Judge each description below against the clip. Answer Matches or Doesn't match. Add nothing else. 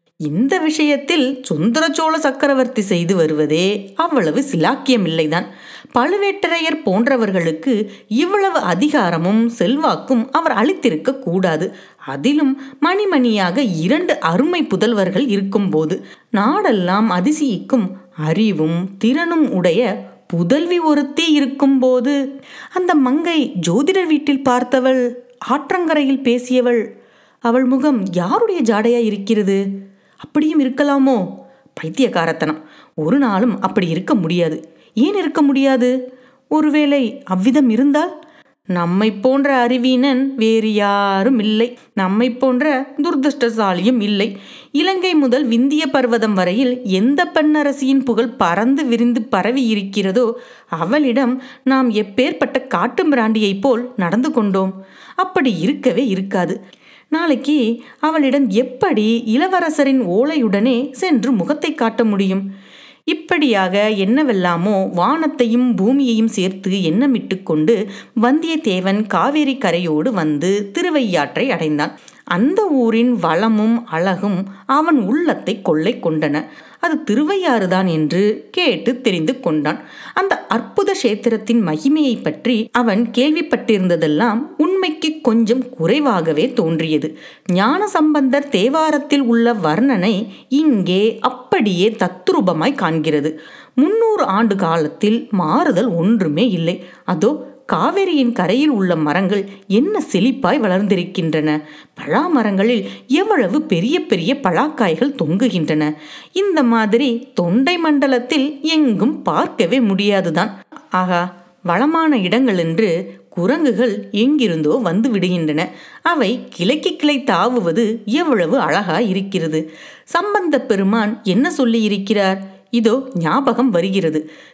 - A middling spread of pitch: Doesn't match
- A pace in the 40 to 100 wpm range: Matches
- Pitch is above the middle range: Matches